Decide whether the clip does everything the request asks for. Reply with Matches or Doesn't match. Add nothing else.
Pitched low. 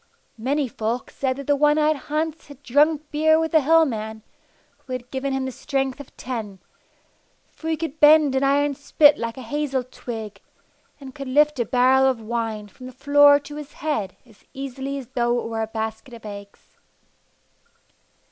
Doesn't match